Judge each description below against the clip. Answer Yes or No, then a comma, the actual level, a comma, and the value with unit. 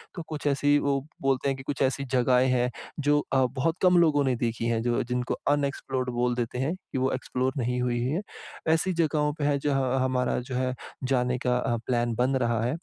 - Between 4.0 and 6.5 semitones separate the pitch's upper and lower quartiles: No, narrow, 2.5 semitones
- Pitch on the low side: Yes, low, 130 Hz